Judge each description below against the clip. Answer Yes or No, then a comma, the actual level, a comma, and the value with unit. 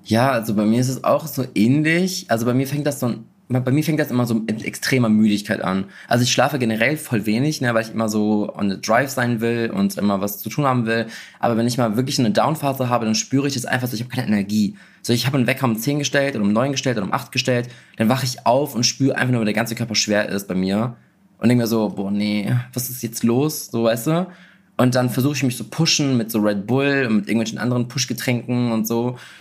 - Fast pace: Yes, fast, 265 wpm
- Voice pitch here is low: Yes, low, 120 Hz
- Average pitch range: Yes, average, 3.2 semitones